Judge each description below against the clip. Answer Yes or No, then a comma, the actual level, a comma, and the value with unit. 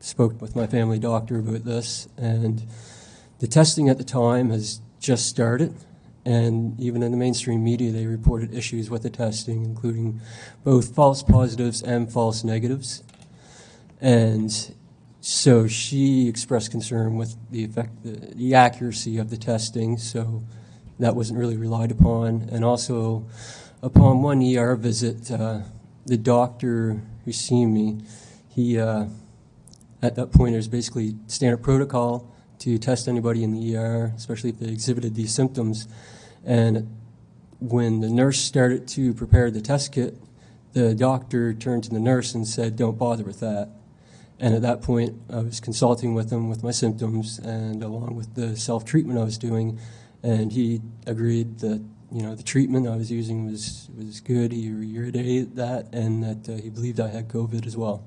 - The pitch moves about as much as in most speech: No, narrow, 1.5 semitones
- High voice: No, low, 115 Hz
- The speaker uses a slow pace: No, average, 160 wpm